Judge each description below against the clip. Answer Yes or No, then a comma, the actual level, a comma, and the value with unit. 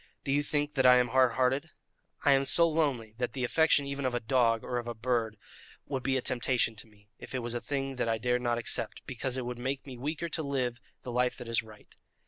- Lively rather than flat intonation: No, narrow, 2.4 semitones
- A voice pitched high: No, low, 125 Hz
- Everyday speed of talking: No, fast, 250 wpm